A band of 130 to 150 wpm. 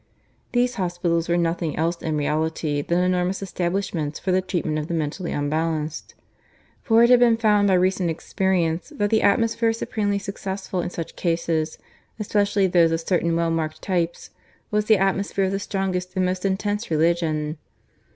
No: average, 165 wpm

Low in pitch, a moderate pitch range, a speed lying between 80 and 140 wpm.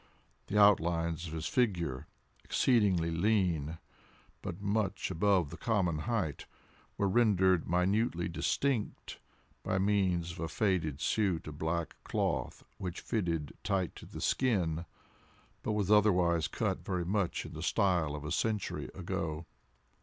Yes: very low, 90 Hz; average, 3.7 semitones; slow, 135 wpm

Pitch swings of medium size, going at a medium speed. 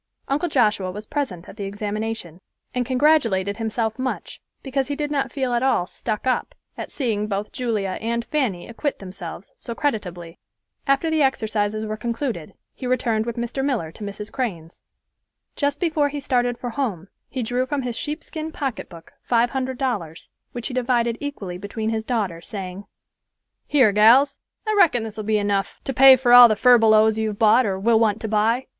Yes: average, 4.1 semitones; average, 180 wpm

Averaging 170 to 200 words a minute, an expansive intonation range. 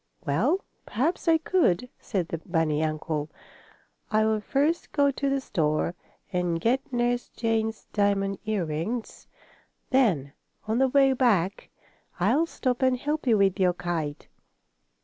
No: slow, 135 wpm; wide, 7.1 semitones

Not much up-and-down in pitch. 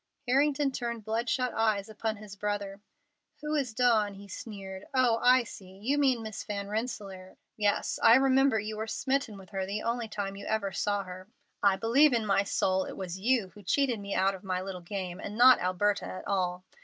No: average, 3.5 semitones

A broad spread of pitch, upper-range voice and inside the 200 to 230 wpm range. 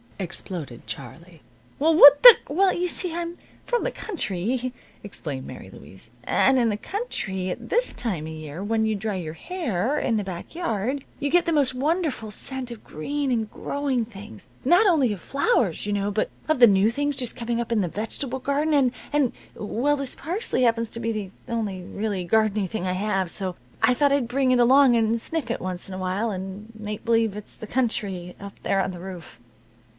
Yes: wide, 6.2 semitones; high, 225 Hz; fast, 205 wpm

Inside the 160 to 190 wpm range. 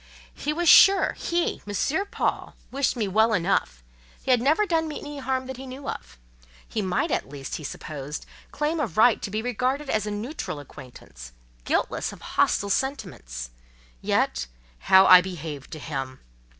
Yes: average, 165 wpm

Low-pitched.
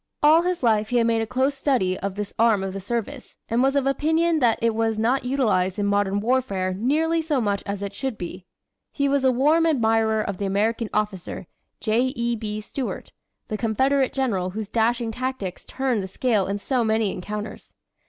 No: high, 225 Hz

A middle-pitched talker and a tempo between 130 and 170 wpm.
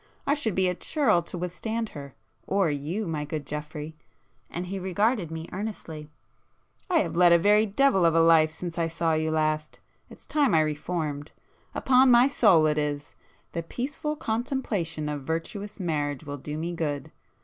Yes: medium, 165 Hz; average, 160 wpm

